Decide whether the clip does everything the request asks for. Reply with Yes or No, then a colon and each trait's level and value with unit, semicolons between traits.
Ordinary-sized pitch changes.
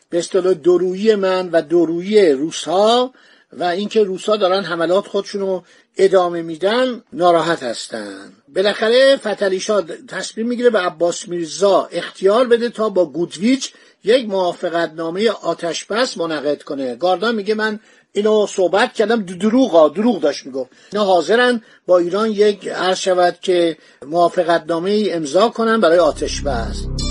Yes: average, 4.3 semitones